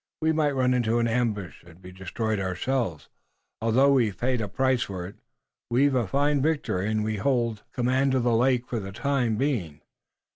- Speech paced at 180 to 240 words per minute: Yes, average, 185 wpm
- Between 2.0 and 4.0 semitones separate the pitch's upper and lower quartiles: No, average, 4.5 semitones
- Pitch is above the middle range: No, low, 120 Hz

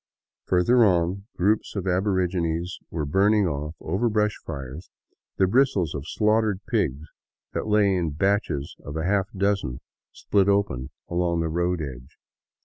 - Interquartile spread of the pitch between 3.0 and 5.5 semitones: Yes, average, 4.1 semitones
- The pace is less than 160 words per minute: Yes, average, 140 wpm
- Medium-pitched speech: No, very low, 90 Hz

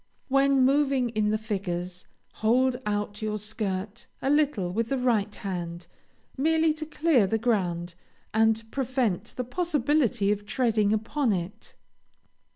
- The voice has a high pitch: Yes, high, 225 Hz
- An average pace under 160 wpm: Yes, slow, 135 wpm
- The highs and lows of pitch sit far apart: No, average, 4.7 semitones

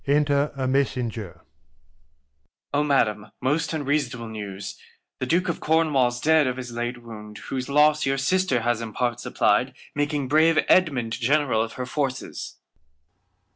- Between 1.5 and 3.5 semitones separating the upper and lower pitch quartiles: No, average, 3.9 semitones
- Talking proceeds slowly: No, average, 145 wpm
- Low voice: Yes, low, 130 Hz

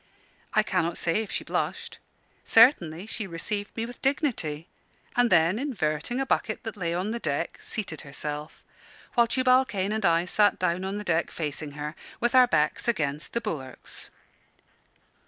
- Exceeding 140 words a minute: Yes, average, 165 wpm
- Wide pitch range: Yes, wide, 6.5 semitones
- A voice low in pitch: No, high, 190 Hz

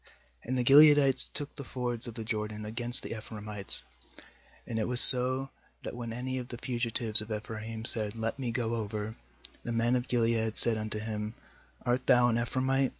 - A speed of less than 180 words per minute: No, average, 185 wpm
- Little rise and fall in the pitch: Yes, narrow, 2.3 semitones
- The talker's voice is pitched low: Yes, low, 115 Hz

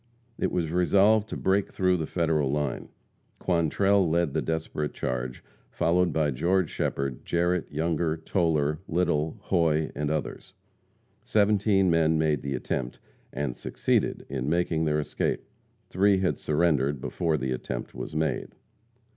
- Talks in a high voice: No, very low, 80 Hz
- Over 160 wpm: No, average, 140 wpm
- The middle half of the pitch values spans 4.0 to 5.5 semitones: No, average, 3.4 semitones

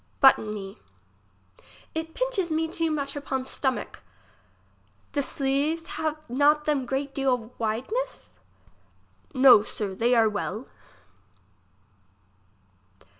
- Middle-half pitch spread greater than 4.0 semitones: Yes, average, 4.5 semitones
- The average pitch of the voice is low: No, very high, 275 Hz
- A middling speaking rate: No, slow, 100 wpm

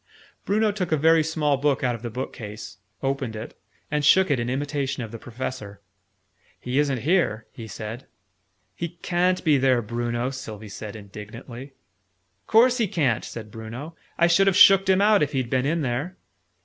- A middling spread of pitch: No, wide, 6.0 semitones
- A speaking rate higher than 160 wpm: Yes, average, 175 wpm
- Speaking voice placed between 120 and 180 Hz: Yes, low, 135 Hz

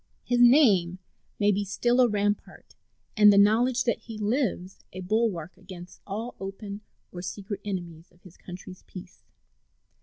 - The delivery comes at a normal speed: Yes, average, 150 wpm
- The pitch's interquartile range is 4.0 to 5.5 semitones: No, average, 3.5 semitones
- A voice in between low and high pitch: No, high, 200 Hz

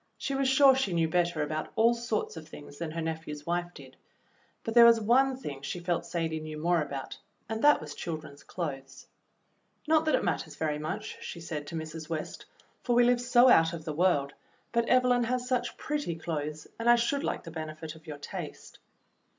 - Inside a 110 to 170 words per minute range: No, fast, 205 wpm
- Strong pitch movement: Yes, wide, 7.5 semitones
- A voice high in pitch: No, medium, 170 Hz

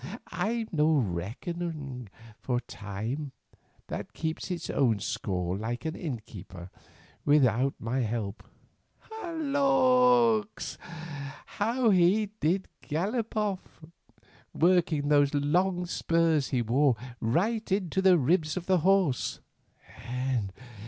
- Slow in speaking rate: Yes, slow, 100 wpm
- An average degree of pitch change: No, wide, 7.2 semitones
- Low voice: No, medium, 160 Hz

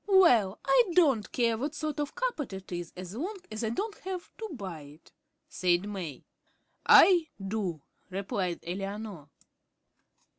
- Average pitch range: No, wide, 8.9 semitones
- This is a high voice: Yes, high, 215 Hz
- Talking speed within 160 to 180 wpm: No, average, 150 wpm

